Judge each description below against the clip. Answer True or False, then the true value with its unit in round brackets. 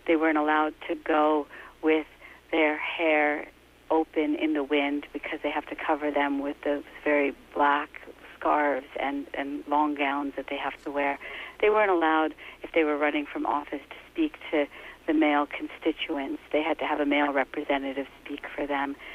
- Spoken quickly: False (180 wpm)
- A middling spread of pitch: False (1.6 semitones)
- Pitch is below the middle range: False (150 Hz)